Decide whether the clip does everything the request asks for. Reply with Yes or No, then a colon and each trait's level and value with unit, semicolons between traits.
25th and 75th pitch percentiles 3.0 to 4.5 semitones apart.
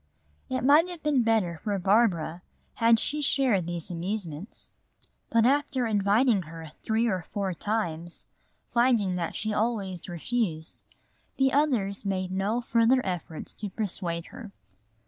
No: average, 5.0 semitones